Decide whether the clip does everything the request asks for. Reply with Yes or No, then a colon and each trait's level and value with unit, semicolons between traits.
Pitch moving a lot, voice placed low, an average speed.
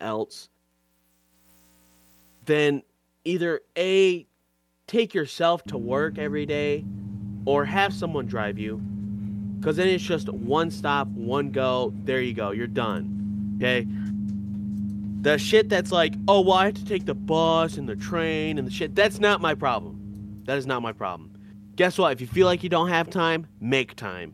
Yes: wide, 8.8 semitones; low, 120 Hz; average, 170 wpm